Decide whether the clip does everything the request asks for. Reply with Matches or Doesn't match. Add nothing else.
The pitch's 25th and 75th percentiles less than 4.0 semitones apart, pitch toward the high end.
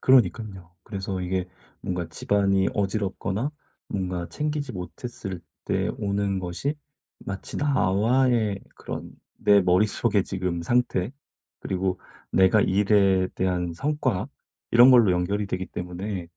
Doesn't match